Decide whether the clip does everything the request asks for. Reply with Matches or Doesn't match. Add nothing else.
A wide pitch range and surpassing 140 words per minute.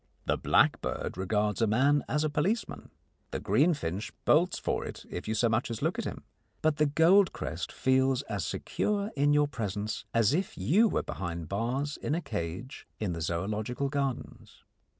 Matches